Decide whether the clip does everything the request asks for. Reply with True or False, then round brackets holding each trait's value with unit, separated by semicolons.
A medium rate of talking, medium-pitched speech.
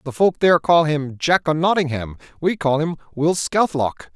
True (190 wpm; 155 Hz)